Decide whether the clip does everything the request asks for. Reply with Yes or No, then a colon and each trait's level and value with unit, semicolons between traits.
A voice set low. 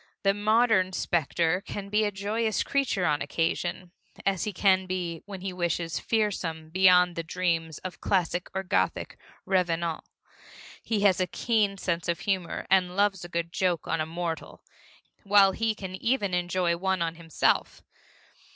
No: medium, 185 Hz